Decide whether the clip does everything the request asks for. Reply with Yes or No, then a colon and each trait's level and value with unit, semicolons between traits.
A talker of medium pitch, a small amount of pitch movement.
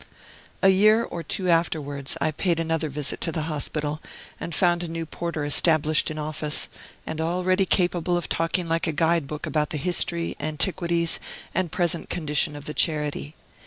Yes: medium, 165 Hz; narrow, 2.3 semitones